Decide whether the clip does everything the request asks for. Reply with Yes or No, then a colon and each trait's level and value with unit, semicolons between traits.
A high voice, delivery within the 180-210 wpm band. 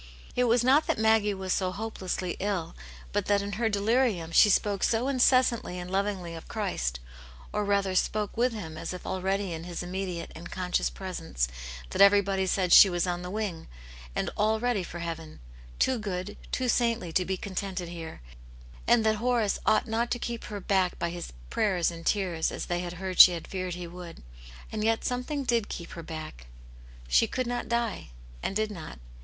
Yes: high, 195 Hz; average, 195 wpm